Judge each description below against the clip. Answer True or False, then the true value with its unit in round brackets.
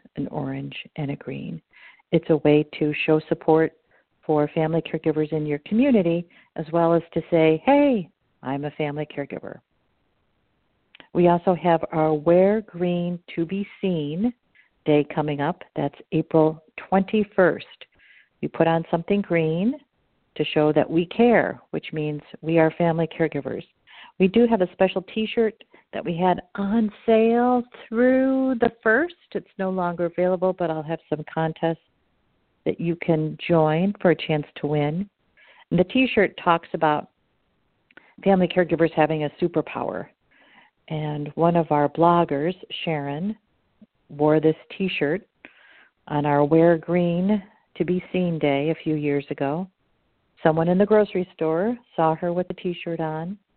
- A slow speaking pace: False (150 wpm)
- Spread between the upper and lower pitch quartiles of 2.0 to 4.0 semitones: True (3.4 semitones)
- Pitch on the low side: False (170 Hz)